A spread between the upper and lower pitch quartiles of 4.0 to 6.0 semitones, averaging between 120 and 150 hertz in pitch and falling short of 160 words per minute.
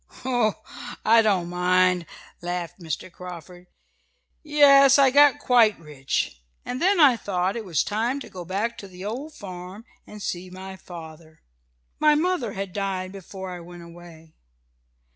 No: average, 5.0 semitones; high, 190 Hz; average, 150 wpm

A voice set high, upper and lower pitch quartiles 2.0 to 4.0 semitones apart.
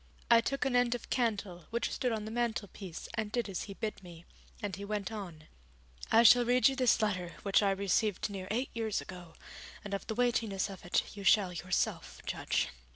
Yes: high, 210 Hz; average, 3.4 semitones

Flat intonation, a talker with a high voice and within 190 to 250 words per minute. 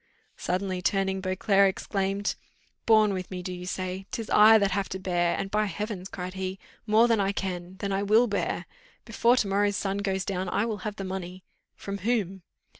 Yes: narrow, 1.7 semitones; high, 195 Hz; average, 195 wpm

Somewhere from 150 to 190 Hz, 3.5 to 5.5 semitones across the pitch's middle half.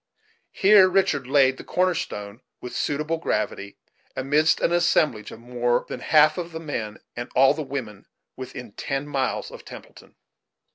No: low, 135 Hz; average, 4.8 semitones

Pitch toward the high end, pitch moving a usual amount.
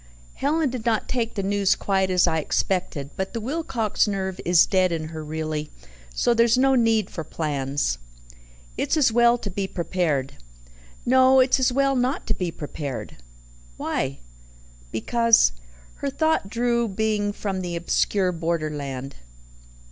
No: high, 195 Hz; wide, 6.7 semitones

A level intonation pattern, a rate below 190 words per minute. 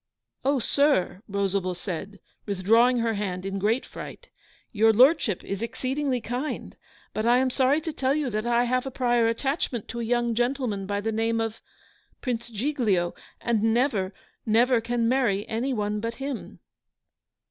No: average, 3.5 semitones; average, 160 wpm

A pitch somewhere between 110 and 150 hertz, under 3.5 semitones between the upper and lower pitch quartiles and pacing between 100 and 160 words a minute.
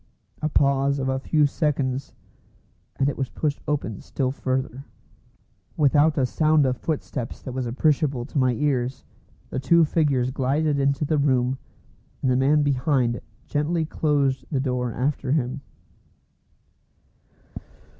Yes: low, 135 Hz; narrow, 2.4 semitones; slow, 135 wpm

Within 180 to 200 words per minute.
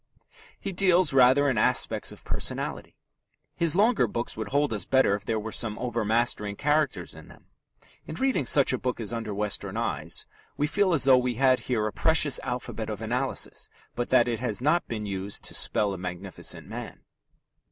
Yes: average, 185 wpm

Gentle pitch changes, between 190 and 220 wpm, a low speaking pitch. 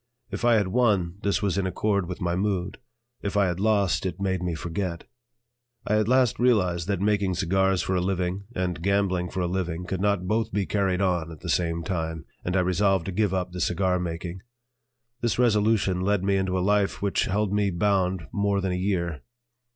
Yes: narrow, 2.2 semitones; fast, 205 wpm; very low, 95 Hz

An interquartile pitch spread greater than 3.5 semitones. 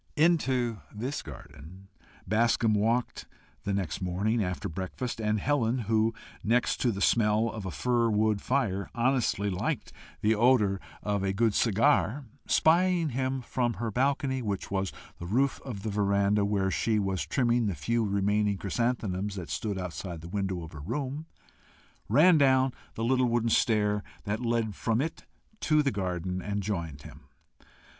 Yes: average, 4.0 semitones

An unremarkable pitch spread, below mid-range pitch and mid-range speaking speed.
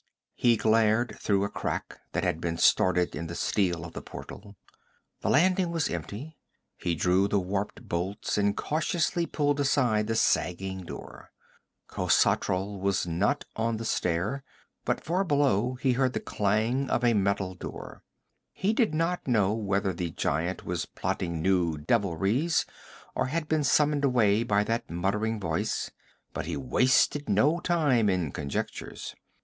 No: wide, 6.6 semitones; low, 105 Hz; average, 155 wpm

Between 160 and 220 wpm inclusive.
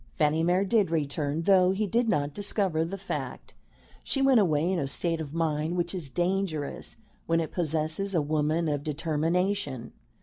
Yes: average, 170 wpm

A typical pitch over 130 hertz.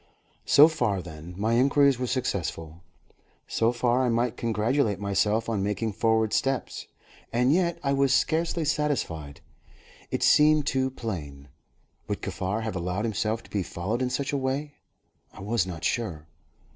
No: low, 115 Hz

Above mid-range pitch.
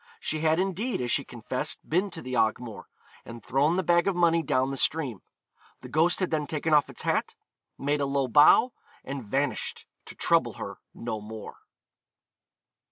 No: medium, 145 Hz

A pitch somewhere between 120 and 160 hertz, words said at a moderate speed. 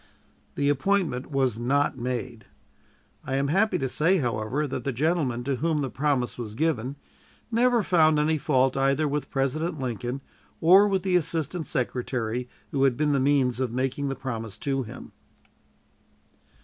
Yes: low, 135 Hz; average, 160 wpm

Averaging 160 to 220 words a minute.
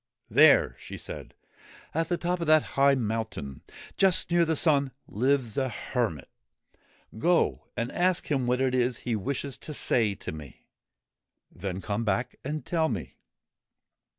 No: average, 150 wpm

